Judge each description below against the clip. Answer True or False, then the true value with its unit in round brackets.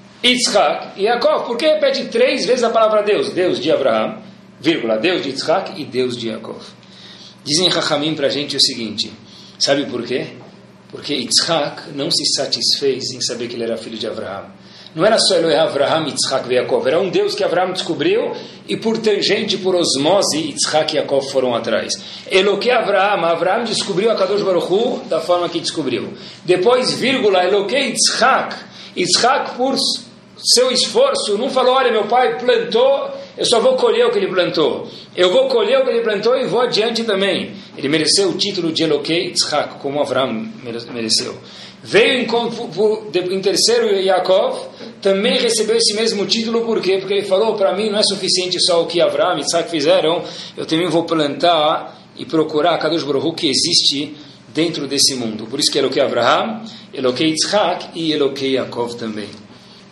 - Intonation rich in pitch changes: True (7.3 semitones)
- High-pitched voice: True (195 Hz)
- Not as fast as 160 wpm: False (175 wpm)